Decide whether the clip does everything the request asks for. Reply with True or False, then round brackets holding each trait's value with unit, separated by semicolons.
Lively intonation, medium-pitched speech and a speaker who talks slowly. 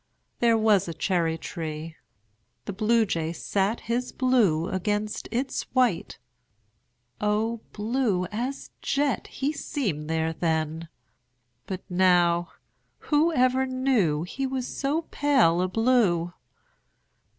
False (6.9 semitones; 210 Hz; 105 wpm)